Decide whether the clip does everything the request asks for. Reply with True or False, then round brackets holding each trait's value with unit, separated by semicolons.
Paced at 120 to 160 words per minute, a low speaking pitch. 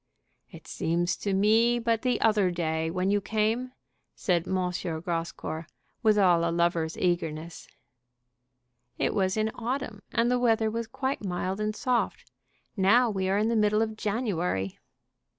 False (150 wpm; 200 Hz)